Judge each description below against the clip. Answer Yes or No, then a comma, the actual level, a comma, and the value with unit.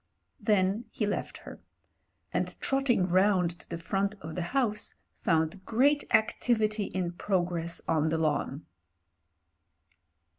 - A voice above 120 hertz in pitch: Yes, high, 190 Hz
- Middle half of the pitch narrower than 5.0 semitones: Yes, average, 4.1 semitones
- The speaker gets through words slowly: Yes, slow, 125 wpm